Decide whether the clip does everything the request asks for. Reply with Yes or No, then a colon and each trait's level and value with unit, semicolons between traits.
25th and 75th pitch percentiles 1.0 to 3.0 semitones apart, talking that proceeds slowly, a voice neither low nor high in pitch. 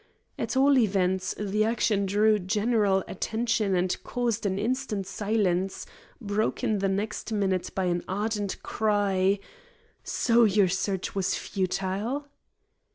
No: narrow, 2.4 semitones; slow, 120 wpm; high, 205 Hz